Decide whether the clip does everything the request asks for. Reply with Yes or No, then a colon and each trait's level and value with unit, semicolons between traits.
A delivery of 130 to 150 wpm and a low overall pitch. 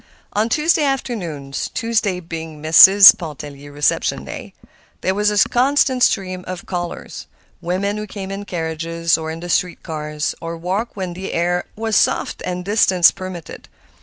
No: average, 140 wpm; medium, 180 Hz